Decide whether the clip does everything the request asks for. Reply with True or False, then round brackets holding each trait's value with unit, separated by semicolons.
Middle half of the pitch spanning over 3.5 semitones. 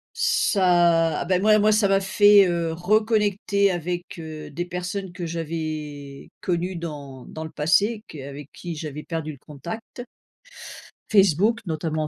True (4.2 semitones)